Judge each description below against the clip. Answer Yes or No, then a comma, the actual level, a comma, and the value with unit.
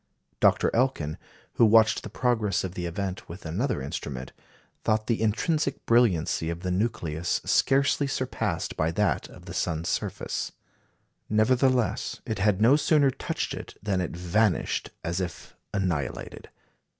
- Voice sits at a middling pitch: No, low, 105 Hz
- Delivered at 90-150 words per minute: Yes, average, 140 wpm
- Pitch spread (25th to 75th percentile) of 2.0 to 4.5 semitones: No, wide, 5.6 semitones